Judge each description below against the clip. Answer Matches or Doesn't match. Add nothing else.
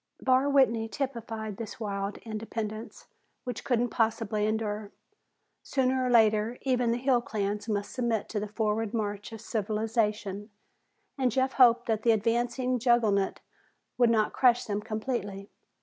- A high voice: Matches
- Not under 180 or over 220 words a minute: Doesn't match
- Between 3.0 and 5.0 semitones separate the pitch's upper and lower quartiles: Doesn't match